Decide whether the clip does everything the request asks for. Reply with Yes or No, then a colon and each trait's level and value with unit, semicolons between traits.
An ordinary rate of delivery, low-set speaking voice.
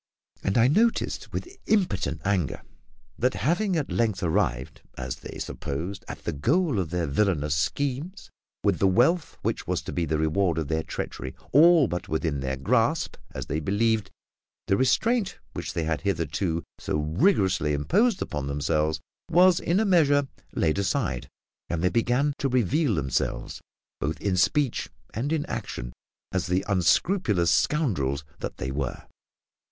Yes: average, 155 wpm; very low, 95 Hz